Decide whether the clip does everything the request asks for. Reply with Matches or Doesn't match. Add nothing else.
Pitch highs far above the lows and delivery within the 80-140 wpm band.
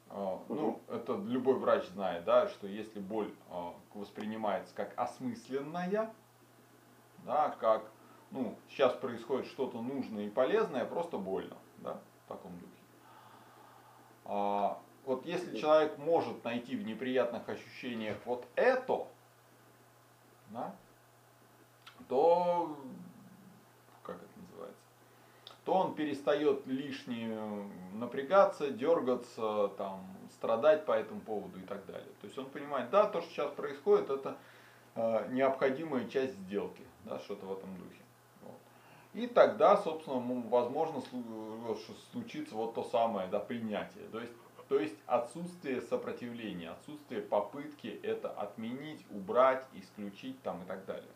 Matches